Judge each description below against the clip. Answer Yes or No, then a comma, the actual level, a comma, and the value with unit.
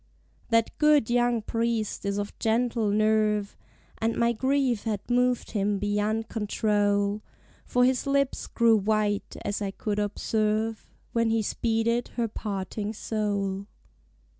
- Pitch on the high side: Yes, high, 220 Hz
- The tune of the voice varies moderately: No, narrow, 2.2 semitones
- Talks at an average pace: No, slow, 130 wpm